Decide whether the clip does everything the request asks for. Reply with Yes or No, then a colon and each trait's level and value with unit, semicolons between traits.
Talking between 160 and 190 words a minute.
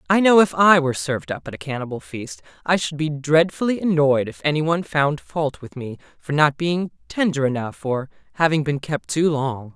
No: fast, 205 wpm